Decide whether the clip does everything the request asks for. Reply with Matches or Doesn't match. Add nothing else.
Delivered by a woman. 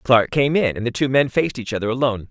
Doesn't match